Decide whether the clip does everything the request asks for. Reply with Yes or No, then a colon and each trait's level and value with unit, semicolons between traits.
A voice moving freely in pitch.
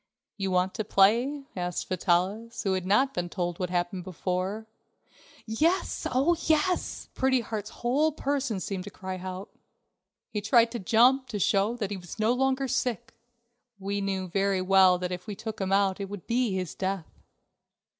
No: average, 4.4 semitones